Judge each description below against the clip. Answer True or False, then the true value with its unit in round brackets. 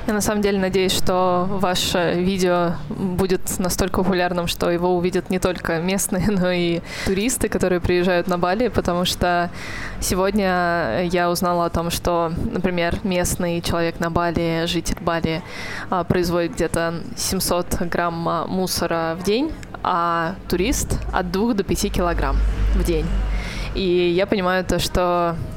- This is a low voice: False (180 Hz)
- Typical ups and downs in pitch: False (1.7 semitones)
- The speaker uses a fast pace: False (140 wpm)